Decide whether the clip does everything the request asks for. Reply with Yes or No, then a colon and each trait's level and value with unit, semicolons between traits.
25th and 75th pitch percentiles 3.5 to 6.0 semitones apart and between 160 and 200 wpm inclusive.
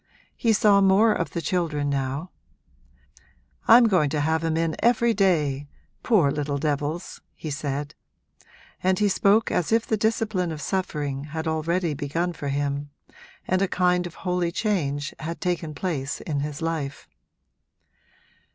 No: average, 4.4 semitones; average, 150 wpm